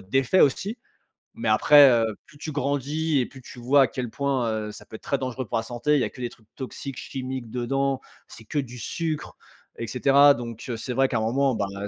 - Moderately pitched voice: No, low, 130 Hz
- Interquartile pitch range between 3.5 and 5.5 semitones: No, average, 2.9 semitones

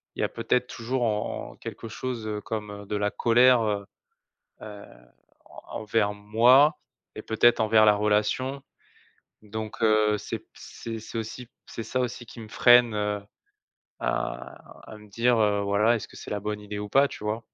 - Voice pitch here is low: Yes, low, 110 Hz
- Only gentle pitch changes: Yes, narrow, 2.3 semitones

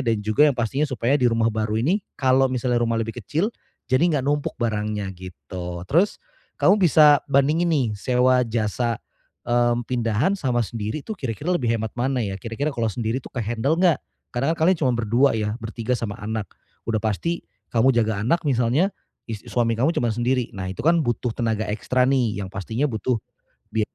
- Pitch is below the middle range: Yes, low, 120 Hz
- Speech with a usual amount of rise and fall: Yes, average, 3.7 semitones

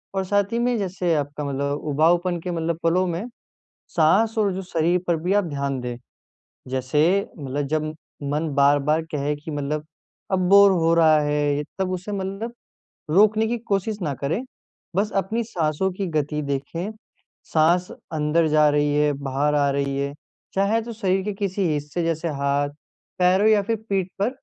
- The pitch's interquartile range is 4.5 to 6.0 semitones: Yes, average, 4.8 semitones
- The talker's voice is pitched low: No, medium, 165 Hz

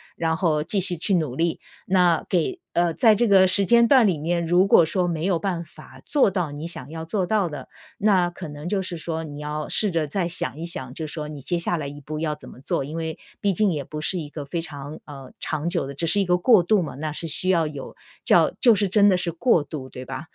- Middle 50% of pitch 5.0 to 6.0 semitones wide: No, average, 3.5 semitones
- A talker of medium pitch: Yes, medium, 165 Hz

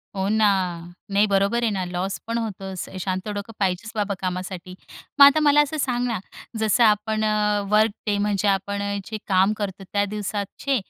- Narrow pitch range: Yes, narrow, 2.2 semitones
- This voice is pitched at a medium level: No, high, 205 Hz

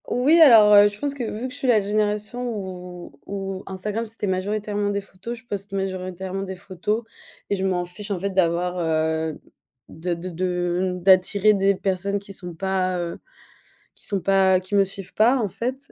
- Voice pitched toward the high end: Yes, high, 195 Hz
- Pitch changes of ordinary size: No, narrow, 2.3 semitones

